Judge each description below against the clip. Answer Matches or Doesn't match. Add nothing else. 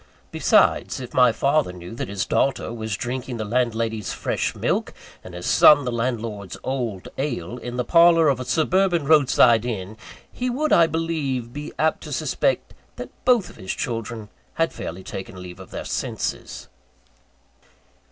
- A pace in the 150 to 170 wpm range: Matches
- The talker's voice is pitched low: Matches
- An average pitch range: Doesn't match